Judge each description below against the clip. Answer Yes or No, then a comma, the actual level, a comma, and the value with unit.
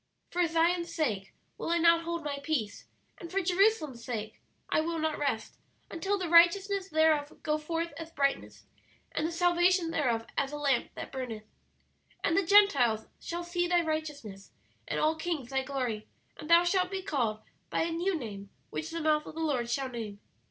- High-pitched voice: Yes, very high, 315 Hz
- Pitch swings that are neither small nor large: Yes, average, 4.6 semitones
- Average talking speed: Yes, average, 185 wpm